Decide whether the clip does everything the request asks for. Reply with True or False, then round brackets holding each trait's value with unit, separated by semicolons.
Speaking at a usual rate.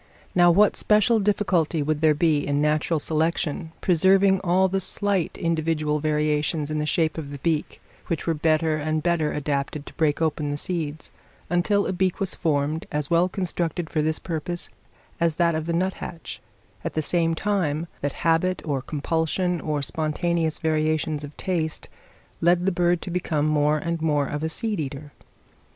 True (170 wpm)